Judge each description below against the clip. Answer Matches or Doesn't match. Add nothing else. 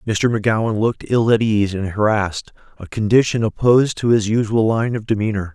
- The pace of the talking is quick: Doesn't match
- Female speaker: Doesn't match